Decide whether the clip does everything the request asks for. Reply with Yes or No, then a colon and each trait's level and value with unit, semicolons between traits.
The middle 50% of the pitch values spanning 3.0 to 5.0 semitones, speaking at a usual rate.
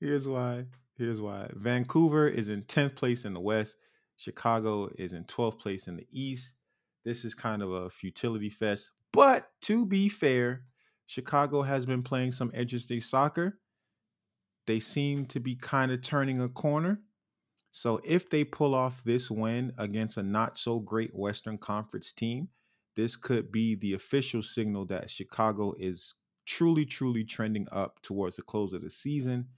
Yes: average, 3.8 semitones; average, 165 wpm